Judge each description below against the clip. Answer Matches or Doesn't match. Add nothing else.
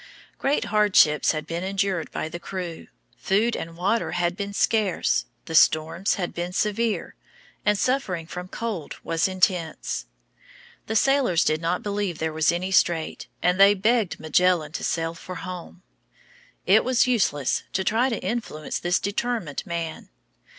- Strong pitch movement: Doesn't match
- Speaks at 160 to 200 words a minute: Doesn't match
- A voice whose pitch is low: Doesn't match